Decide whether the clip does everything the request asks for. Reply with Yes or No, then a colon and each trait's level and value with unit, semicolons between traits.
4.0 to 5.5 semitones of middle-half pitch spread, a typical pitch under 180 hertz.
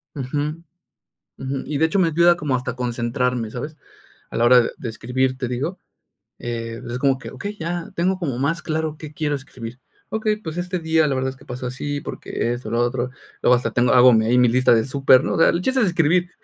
Yes: average, 4.5 semitones; low, 135 Hz